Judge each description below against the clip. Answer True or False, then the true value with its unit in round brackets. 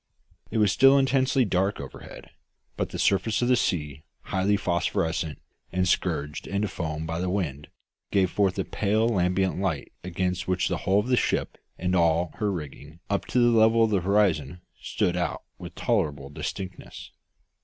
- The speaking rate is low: False (170 wpm)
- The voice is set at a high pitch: False (95 Hz)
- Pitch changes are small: False (3.9 semitones)